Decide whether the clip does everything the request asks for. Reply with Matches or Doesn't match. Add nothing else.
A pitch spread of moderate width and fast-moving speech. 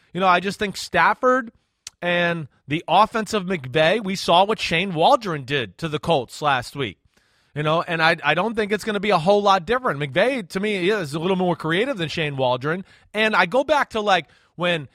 Matches